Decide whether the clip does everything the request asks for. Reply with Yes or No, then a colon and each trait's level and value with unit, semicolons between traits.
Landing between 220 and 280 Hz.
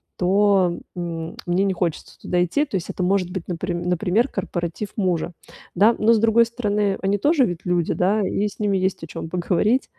No: high, 190 Hz